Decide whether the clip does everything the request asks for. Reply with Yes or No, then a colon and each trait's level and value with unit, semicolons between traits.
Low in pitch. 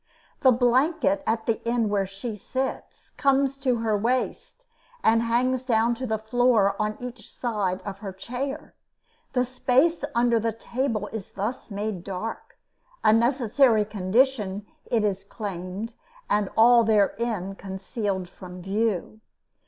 No: high, 225 Hz